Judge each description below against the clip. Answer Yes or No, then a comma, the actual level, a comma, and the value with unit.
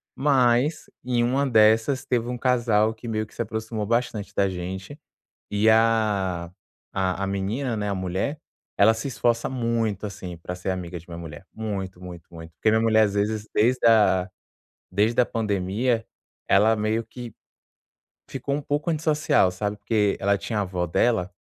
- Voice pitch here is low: Yes, low, 110 Hz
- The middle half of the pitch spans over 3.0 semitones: Yes, average, 3.5 semitones